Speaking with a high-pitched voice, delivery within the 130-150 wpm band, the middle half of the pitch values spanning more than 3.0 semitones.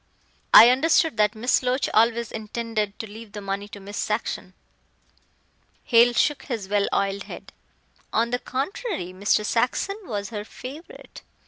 Yes: high, 225 Hz; average, 145 wpm; average, 3.4 semitones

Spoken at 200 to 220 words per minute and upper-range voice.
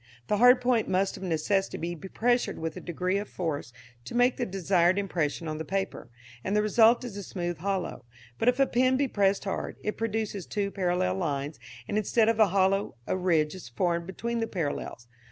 Yes: fast, 205 wpm; high, 195 Hz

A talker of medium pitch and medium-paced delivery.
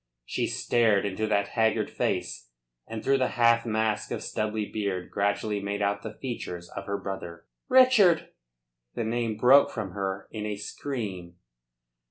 No: low, 105 Hz; average, 155 wpm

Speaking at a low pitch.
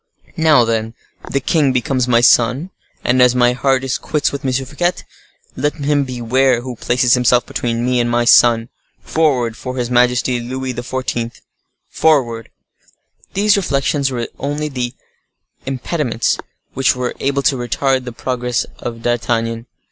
Yes: low, 125 Hz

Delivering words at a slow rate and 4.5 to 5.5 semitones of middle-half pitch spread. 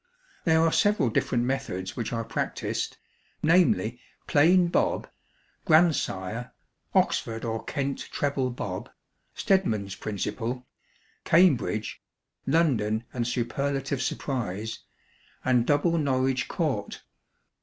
Yes: slow, 95 wpm; average, 4.9 semitones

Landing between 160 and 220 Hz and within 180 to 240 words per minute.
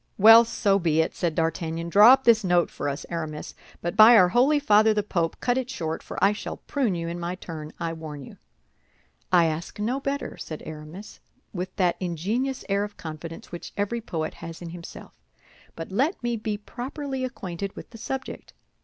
Yes: high, 190 Hz; average, 195 wpm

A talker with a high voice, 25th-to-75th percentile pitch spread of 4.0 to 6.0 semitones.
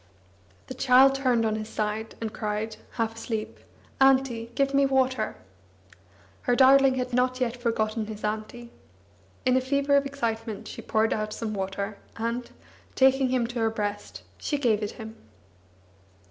No: high, 235 Hz; average, 3.1 semitones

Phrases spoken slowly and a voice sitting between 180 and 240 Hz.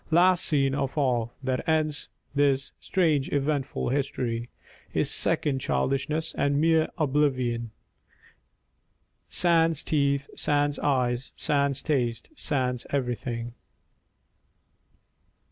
No: slow, 95 wpm; medium, 140 Hz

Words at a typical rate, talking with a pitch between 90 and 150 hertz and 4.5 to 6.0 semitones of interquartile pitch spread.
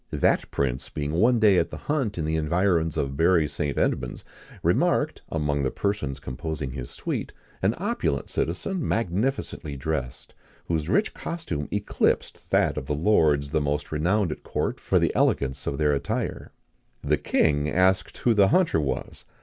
No: average, 165 wpm; very low, 80 Hz; average, 5.3 semitones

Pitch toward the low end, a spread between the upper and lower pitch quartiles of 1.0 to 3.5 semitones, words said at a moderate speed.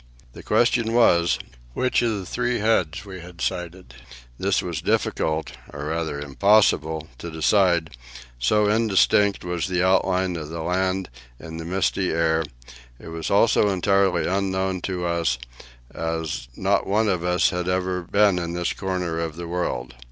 Yes: very low, 90 Hz; average, 2.9 semitones; average, 160 wpm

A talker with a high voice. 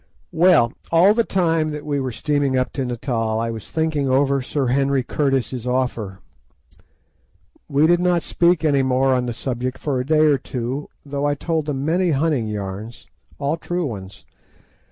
No: medium, 140 Hz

